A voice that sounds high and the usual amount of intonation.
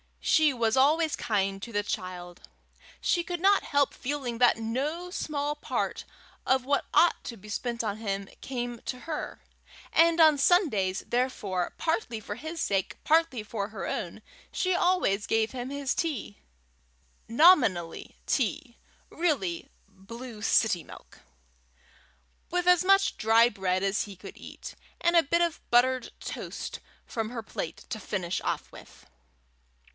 No: high, 245 Hz; wide, 7.2 semitones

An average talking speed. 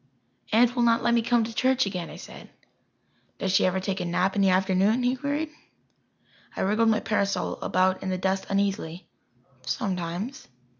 Yes: average, 180 wpm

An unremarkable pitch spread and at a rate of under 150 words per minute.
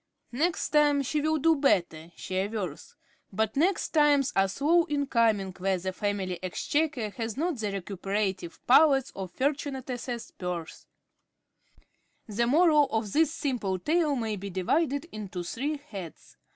No: wide, 7.2 semitones; average, 140 wpm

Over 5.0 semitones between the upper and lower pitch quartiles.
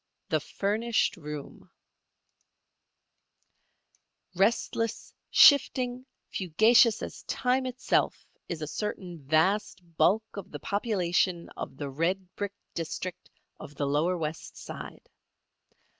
Yes: wide, 5.5 semitones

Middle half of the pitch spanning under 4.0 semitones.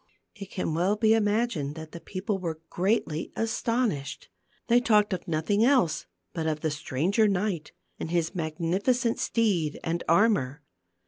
No: wide, 5.4 semitones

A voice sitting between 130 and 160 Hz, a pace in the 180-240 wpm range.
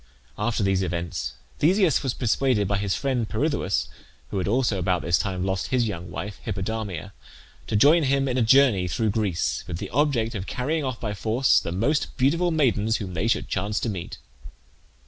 No: low, 110 Hz; average, 185 wpm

